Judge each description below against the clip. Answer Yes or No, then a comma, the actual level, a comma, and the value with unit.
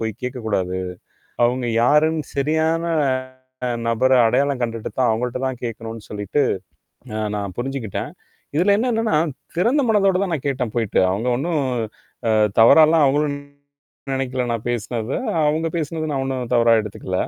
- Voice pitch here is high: No, low, 130 Hz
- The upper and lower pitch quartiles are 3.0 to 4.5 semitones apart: No, average, 5.2 semitones